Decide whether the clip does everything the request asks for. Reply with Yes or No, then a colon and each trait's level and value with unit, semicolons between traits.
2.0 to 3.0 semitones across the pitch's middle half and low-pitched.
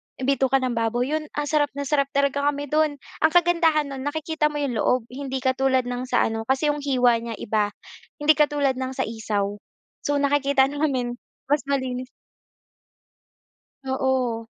No: average, 2.7 semitones; very high, 270 Hz